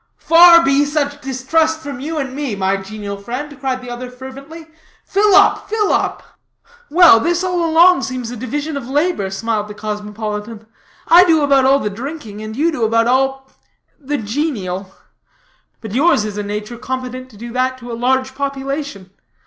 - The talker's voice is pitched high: Yes, very high, 260 Hz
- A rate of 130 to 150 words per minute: No, average, 175 wpm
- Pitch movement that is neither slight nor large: Yes, average, 5.0 semitones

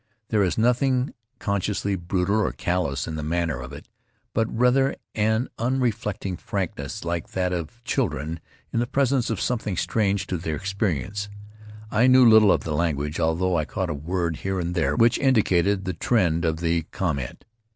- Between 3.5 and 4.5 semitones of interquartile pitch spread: No, average, 5.1 semitones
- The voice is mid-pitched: No, very low, 95 Hz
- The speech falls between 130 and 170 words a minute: No, average, 180 wpm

